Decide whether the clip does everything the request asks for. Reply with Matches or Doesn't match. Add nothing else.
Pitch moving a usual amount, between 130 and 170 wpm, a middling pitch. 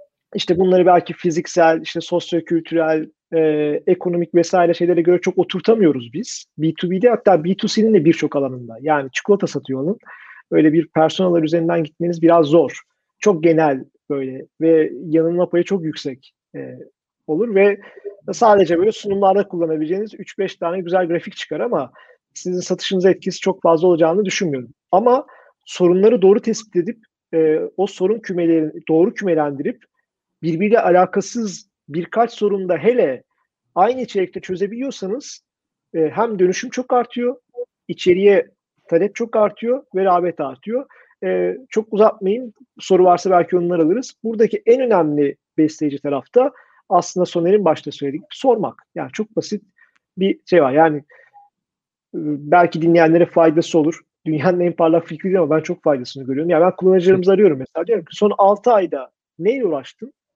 Matches